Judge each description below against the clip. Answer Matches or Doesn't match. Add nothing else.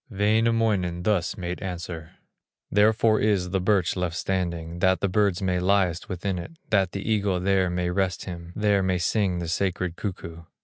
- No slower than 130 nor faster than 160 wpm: Doesn't match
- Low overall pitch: Matches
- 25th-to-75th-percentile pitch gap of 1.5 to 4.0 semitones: Matches